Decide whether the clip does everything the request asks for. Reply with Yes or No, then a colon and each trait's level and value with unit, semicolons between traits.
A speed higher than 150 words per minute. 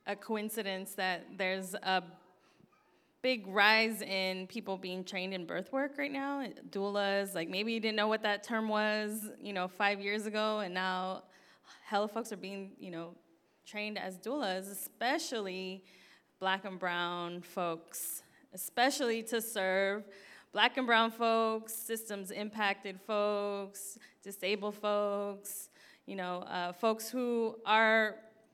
No: slow, 135 wpm